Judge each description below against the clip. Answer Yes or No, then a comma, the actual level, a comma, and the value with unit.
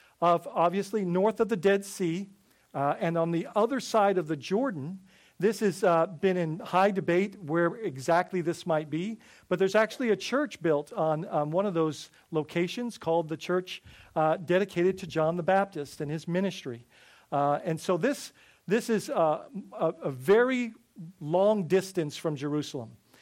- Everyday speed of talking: Yes, average, 170 wpm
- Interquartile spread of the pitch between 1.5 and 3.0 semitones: No, average, 3.7 semitones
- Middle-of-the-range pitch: Yes, medium, 175 Hz